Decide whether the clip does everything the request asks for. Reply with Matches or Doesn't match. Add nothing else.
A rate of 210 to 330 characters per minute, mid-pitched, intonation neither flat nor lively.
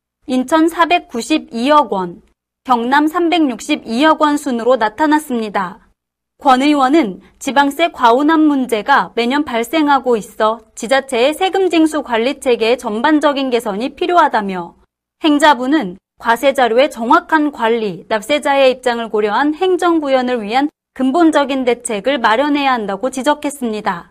Doesn't match